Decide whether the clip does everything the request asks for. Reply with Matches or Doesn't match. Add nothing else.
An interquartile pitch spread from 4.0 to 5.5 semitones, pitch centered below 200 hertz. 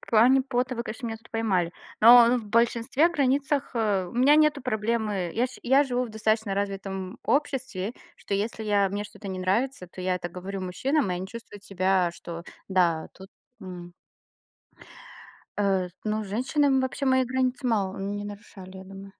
Doesn't match